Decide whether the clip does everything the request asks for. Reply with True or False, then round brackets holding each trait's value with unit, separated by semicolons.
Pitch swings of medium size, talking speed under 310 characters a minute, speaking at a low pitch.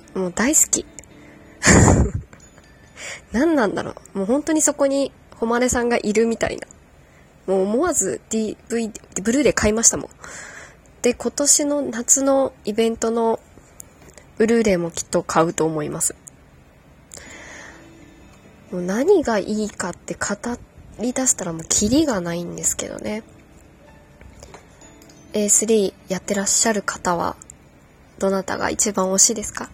False (4.0 semitones; 250 characters per minute; 225 Hz)